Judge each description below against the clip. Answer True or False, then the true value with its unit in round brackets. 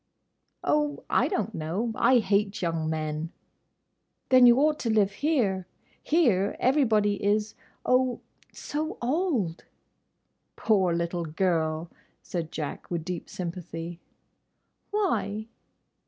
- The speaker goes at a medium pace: False (95 wpm)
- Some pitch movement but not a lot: False (6.8 semitones)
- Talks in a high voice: True (200 Hz)